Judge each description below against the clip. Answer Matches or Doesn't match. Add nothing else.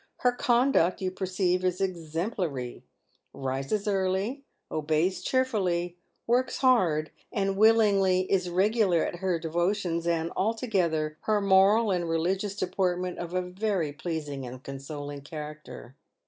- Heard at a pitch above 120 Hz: Matches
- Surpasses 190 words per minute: Doesn't match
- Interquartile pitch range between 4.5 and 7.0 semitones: Doesn't match